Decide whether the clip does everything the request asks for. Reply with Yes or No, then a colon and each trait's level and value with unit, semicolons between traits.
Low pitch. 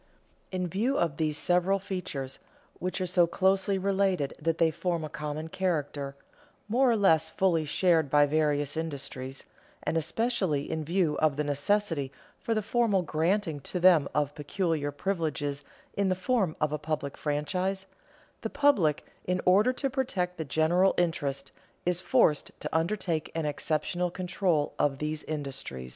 No: medium, 165 Hz